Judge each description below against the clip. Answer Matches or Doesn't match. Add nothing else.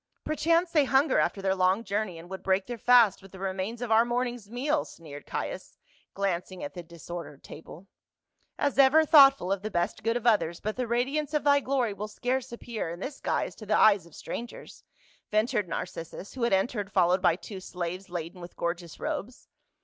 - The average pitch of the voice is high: Matches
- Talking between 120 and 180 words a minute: Doesn't match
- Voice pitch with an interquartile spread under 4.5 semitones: Doesn't match